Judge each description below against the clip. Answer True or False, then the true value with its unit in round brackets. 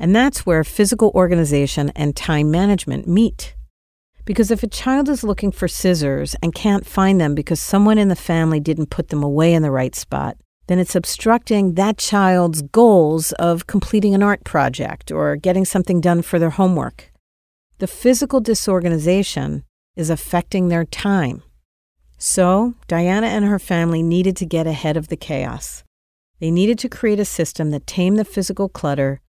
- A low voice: False (175 Hz)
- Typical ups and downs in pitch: True (4.9 semitones)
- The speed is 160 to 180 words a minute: True (170 wpm)